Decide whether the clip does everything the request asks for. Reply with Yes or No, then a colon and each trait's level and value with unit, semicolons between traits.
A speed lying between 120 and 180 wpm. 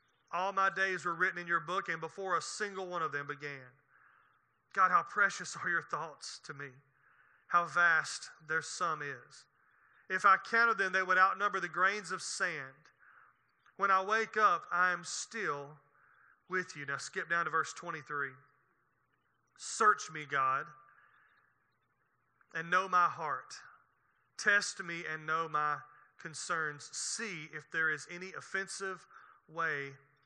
Yes: average, 150 wpm